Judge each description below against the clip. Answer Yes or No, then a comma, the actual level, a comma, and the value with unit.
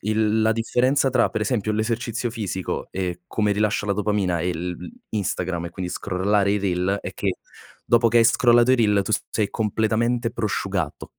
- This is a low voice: Yes, low, 105 Hz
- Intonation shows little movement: No, average, 3.4 semitones